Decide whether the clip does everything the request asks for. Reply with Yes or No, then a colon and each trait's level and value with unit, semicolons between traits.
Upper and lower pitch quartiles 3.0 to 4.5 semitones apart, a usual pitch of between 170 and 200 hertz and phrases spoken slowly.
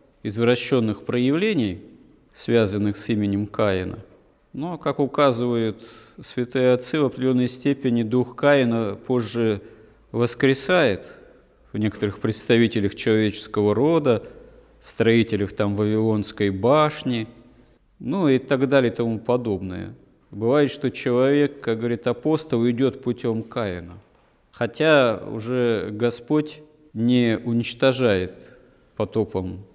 No: average, 3.7 semitones; low, 120 Hz; slow, 100 wpm